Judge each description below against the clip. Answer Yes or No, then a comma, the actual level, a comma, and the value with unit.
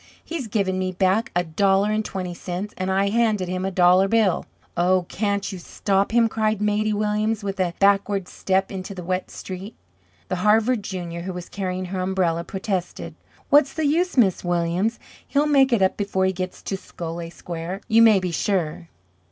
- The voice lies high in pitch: Yes, high, 195 Hz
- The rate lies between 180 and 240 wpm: Yes, average, 185 wpm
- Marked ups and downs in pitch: No, narrow, 2.6 semitones